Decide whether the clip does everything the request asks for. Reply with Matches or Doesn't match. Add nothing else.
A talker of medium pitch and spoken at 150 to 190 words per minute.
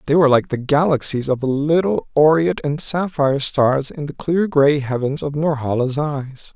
Matches